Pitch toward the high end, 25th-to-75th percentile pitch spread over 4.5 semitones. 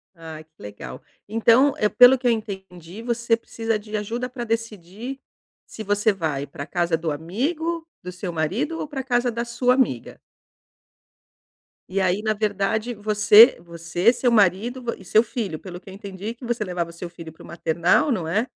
Yes: high, 210 Hz; average, 5.3 semitones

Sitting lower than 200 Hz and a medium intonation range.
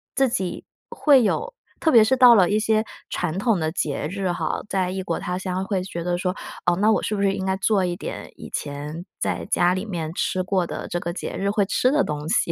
Yes: high, 190 Hz; average, 3.4 semitones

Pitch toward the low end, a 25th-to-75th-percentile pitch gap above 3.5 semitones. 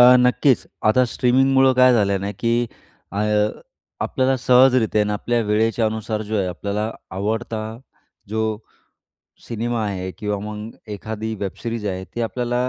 No: low, 110 Hz; average, 2.8 semitones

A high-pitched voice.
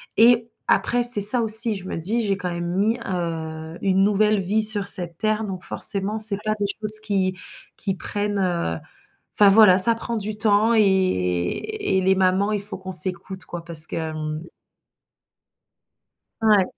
Yes: high, 195 Hz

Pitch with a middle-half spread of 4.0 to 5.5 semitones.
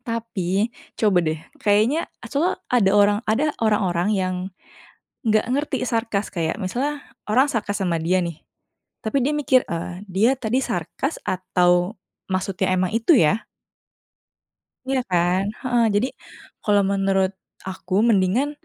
Yes: average, 4.7 semitones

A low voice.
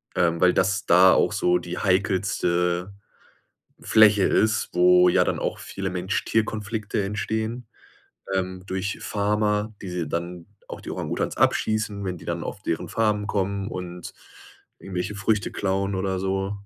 Yes: very low, 95 Hz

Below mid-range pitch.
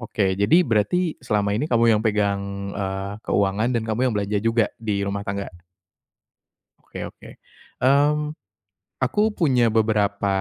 Yes: low, 105 Hz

